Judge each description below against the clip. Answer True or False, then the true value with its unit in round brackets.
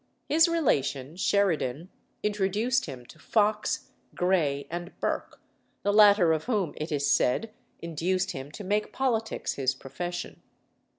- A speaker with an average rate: False (130 wpm)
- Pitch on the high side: False (180 Hz)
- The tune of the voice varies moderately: False (6.2 semitones)